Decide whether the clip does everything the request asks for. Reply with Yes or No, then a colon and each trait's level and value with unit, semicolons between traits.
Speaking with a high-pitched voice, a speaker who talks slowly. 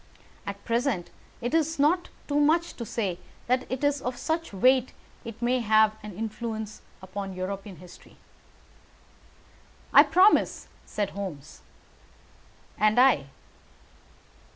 Yes: high, 230 Hz; slow, 125 wpm